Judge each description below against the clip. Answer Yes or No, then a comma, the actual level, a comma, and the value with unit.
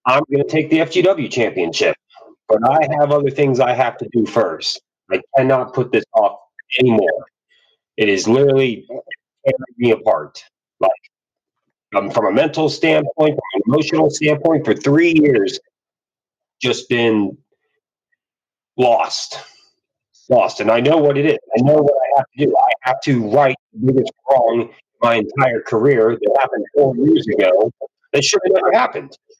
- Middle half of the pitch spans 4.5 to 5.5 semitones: No, average, 3.6 semitones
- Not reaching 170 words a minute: Yes, average, 160 wpm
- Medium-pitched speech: Yes, medium, 145 Hz